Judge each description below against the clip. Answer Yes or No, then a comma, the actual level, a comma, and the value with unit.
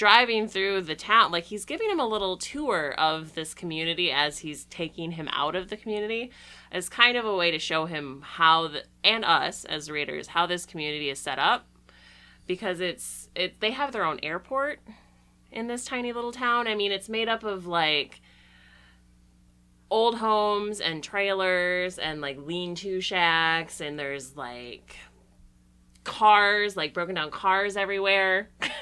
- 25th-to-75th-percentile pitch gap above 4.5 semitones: Yes, wide, 5.6 semitones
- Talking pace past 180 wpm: No, average, 165 wpm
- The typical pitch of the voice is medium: Yes, medium, 175 Hz